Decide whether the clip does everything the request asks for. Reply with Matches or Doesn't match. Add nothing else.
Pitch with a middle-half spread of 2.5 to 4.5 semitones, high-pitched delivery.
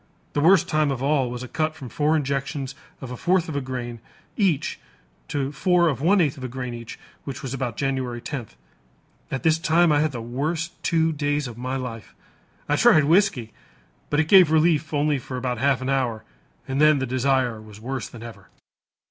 Doesn't match